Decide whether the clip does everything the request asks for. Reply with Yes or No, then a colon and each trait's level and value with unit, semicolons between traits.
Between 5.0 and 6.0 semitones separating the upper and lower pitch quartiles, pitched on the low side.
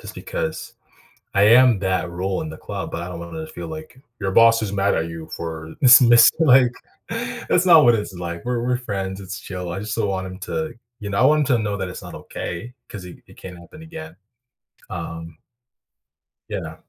Yes: wide, 5.6 semitones; low, 100 Hz